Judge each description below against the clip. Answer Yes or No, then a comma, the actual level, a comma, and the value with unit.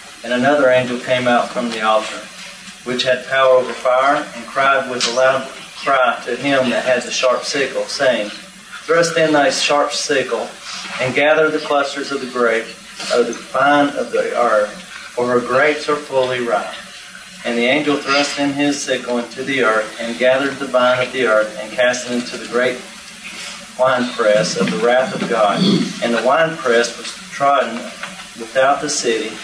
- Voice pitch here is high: No, low, 125 Hz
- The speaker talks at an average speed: Yes, average, 180 wpm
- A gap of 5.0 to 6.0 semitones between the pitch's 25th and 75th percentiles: No, average, 2.7 semitones